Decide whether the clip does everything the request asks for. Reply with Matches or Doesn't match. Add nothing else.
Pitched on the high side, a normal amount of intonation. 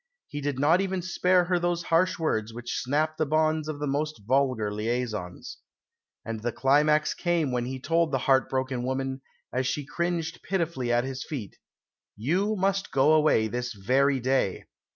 Doesn't match